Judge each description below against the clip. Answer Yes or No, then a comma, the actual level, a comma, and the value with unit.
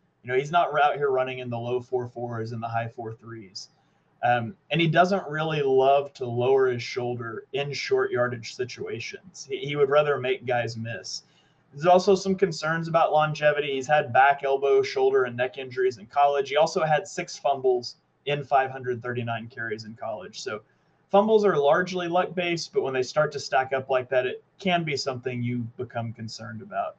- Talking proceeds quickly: No, average, 195 wpm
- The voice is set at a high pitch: No, medium, 140 Hz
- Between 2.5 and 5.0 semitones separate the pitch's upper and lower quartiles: No, wide, 5.4 semitones